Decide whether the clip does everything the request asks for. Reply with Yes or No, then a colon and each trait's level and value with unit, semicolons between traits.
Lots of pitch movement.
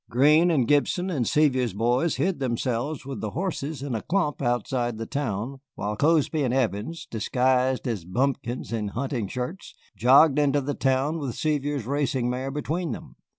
No: average, 3.5 semitones